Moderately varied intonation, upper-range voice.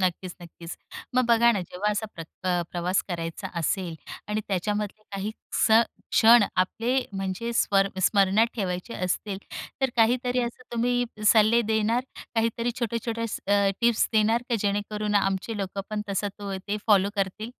Yes: average, 3.2 semitones; high, 210 Hz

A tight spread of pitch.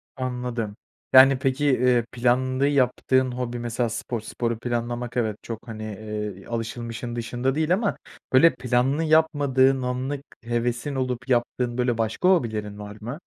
Yes: narrow, 2.0 semitones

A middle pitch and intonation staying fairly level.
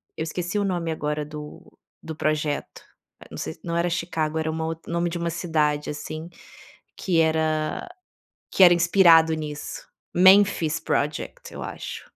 Yes: medium, 160 Hz; narrow, 1.9 semitones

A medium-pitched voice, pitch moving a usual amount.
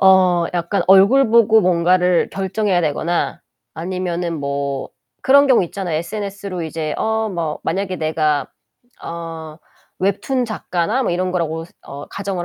Yes: medium, 180 Hz; average, 3.3 semitones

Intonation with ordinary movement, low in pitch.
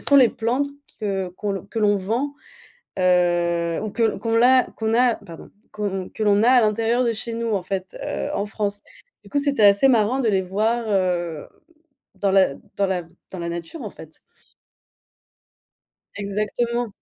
No: average, 3.7 semitones; high, 210 Hz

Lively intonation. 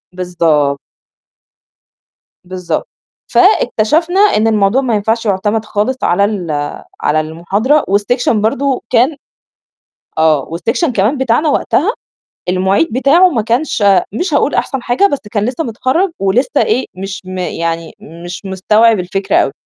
Yes: wide, 5.8 semitones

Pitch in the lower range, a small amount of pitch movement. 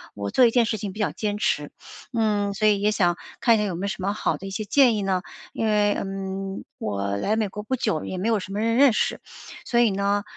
No: high, 205 Hz; narrow, 2.2 semitones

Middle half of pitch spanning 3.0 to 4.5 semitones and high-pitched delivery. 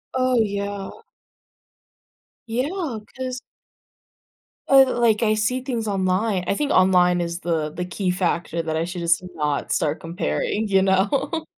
No: average, 5.1 semitones; high, 195 Hz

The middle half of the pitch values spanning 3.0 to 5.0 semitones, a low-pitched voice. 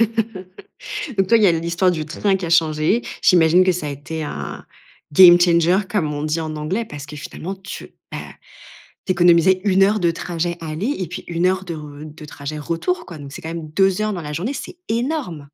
No: average, 3.6 semitones; medium, 170 Hz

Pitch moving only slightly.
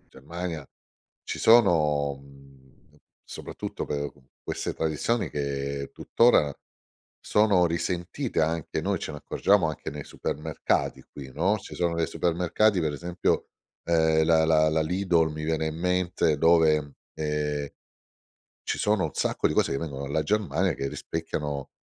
No: average, 3.2 semitones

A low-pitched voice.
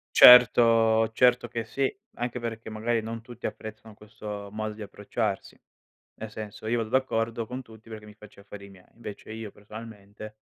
Yes: low, 110 Hz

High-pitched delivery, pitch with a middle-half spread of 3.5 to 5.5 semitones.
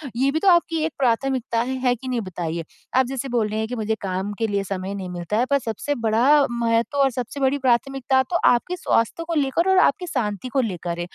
Yes: high, 240 Hz; average, 4.7 semitones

